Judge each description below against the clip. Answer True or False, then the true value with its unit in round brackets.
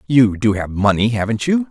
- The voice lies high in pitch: False (115 Hz)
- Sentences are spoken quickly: True (210 wpm)